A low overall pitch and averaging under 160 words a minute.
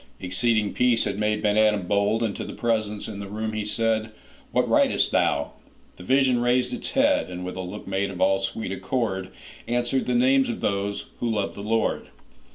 No: low, 110 Hz; average, 175 wpm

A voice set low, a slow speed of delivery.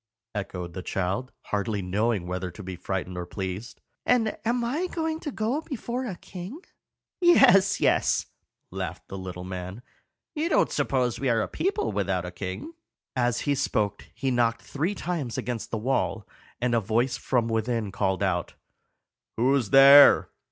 No: low, 115 Hz; average, 160 wpm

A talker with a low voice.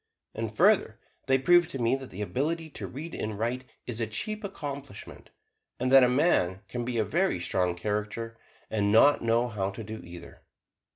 Yes: low, 120 Hz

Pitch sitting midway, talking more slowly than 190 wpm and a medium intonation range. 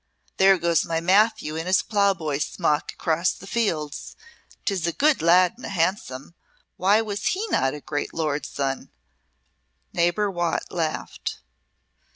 Yes: medium, 170 Hz; average, 145 wpm; average, 4.0 semitones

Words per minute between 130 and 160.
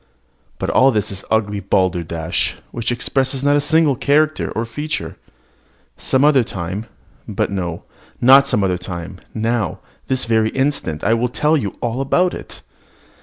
Yes: average, 155 wpm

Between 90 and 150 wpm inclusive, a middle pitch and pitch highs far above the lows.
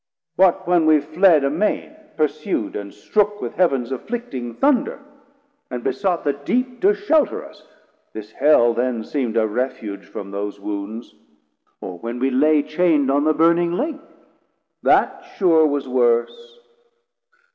Yes: average, 140 wpm; medium, 145 Hz; wide, 7.2 semitones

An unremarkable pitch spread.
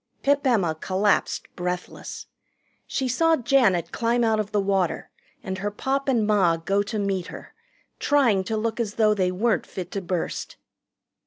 Yes: average, 4.0 semitones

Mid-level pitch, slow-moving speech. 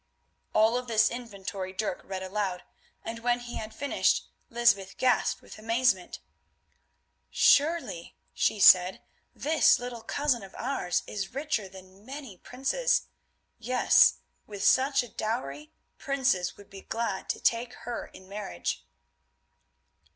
No: high, 225 Hz; slow, 130 wpm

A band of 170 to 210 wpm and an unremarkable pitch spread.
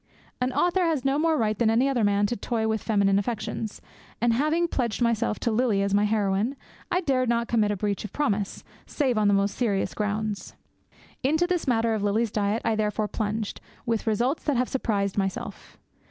Yes: average, 195 wpm; average, 3.6 semitones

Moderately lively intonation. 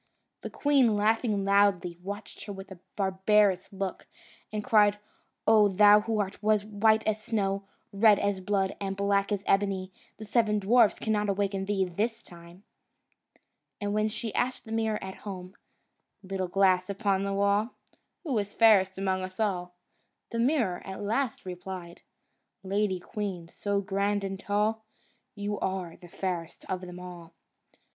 No: narrow, 2.0 semitones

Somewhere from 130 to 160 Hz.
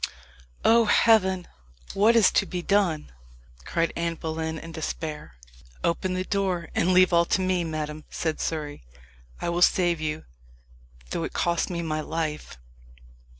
No: medium, 170 Hz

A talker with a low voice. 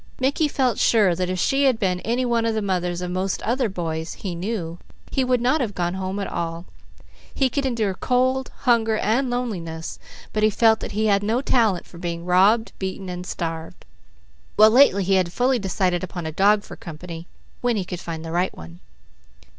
No: high, 195 Hz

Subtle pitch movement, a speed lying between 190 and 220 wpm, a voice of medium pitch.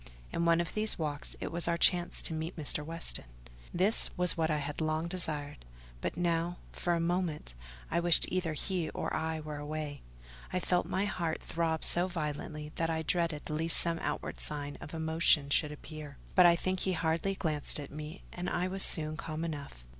Yes: narrow, 2.3 semitones; average, 195 wpm; medium, 165 Hz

